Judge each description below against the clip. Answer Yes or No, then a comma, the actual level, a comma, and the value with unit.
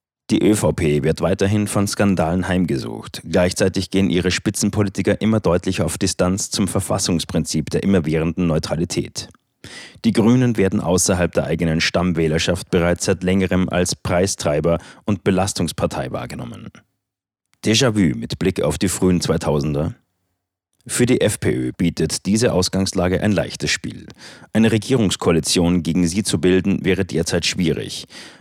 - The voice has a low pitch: Yes, very low, 90 Hz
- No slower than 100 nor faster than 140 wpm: Yes, average, 130 wpm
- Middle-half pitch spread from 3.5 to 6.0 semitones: No, narrow, 2.6 semitones